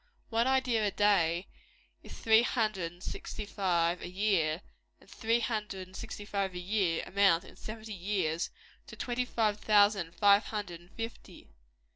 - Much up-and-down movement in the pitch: No, average, 3.6 semitones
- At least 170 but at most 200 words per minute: No, average, 160 wpm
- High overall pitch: Yes, high, 205 Hz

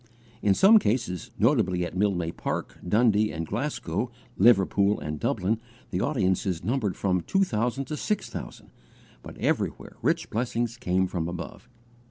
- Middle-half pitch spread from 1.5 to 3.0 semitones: No, average, 4.8 semitones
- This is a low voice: Yes, low, 105 Hz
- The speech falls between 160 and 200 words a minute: No, average, 145 wpm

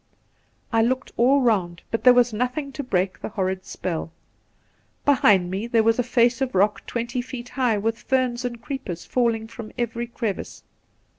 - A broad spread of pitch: No, average, 3.0 semitones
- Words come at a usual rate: Yes, average, 170 wpm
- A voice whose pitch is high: Yes, high, 235 Hz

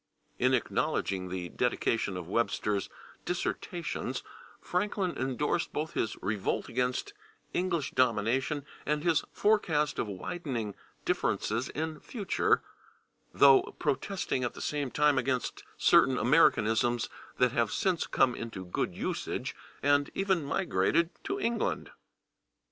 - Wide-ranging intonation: Yes, wide, 6.4 semitones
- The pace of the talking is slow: Yes, slow, 115 wpm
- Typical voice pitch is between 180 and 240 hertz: No, low, 135 Hz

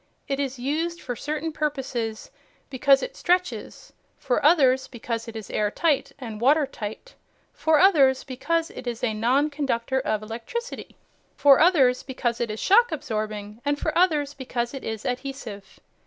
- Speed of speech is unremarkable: Yes, average, 155 wpm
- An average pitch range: Yes, average, 4.5 semitones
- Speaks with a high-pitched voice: Yes, very high, 265 Hz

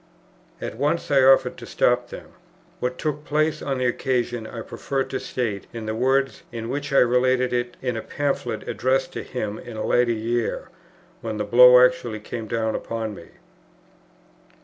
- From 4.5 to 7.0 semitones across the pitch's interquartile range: No, average, 2.8 semitones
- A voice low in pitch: Yes, low, 125 Hz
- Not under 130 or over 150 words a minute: No, average, 175 wpm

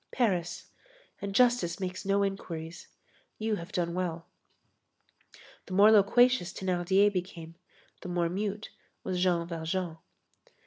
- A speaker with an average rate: No, slow, 120 wpm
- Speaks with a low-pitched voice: No, medium, 185 Hz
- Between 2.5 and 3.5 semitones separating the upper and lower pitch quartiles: Yes, average, 2.8 semitones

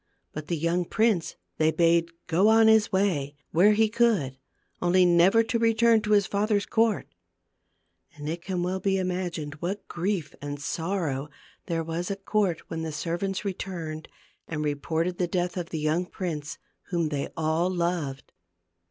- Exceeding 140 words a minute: Yes, average, 160 wpm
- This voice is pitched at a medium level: Yes, medium, 175 Hz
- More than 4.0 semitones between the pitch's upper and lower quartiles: No, average, 3.7 semitones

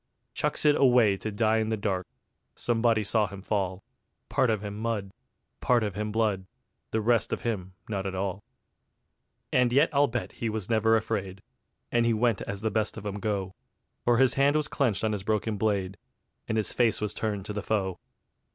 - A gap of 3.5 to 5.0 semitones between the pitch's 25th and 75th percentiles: No, narrow, 2.6 semitones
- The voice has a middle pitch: No, low, 110 Hz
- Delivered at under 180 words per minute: No, average, 195 wpm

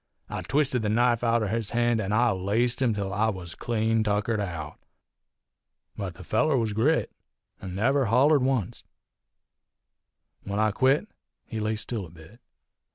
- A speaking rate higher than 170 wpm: No, average, 160 wpm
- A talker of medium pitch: No, low, 110 Hz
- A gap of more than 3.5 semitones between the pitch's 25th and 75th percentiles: No, average, 3.2 semitones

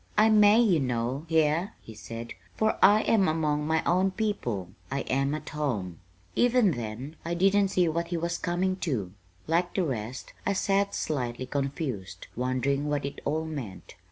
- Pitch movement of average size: No, wide, 6.4 semitones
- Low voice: No, medium, 155 Hz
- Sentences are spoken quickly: No, average, 170 wpm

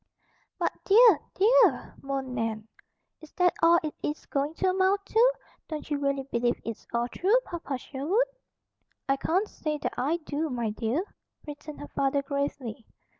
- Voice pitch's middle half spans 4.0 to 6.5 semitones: Yes, average, 5.1 semitones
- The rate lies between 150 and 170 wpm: Yes, average, 160 wpm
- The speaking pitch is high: Yes, very high, 290 Hz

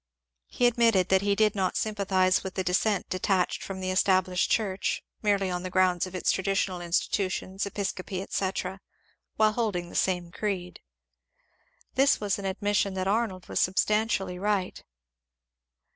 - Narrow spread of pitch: Yes, narrow, 1.9 semitones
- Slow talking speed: No, average, 145 wpm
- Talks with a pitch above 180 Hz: Yes, high, 190 Hz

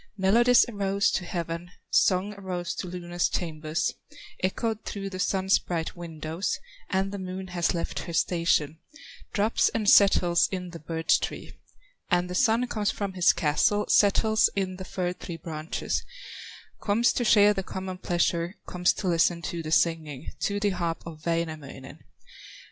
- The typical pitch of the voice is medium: Yes, medium, 180 Hz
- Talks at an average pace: Yes, average, 155 wpm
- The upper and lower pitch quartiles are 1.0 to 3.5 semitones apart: Yes, average, 2.9 semitones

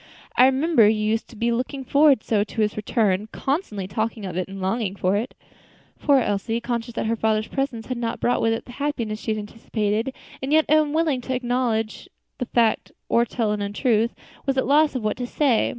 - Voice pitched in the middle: No, high, 230 Hz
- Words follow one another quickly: Yes, fast, 215 wpm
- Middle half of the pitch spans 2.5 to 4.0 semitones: Yes, average, 3.5 semitones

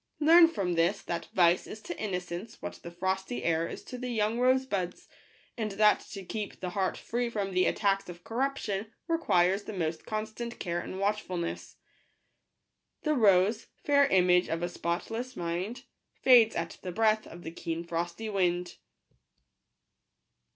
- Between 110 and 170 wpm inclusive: Yes, average, 165 wpm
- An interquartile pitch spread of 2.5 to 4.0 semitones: No, average, 4.4 semitones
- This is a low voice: No, high, 195 Hz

